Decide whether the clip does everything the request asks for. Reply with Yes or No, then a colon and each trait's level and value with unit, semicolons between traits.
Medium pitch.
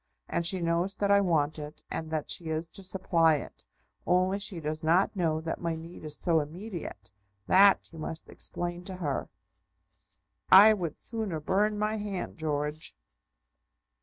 Yes: medium, 170 Hz